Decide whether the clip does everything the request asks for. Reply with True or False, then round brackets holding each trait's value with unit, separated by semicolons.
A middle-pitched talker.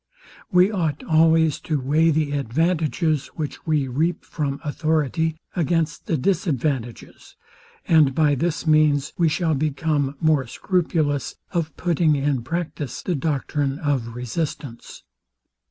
True (155 Hz)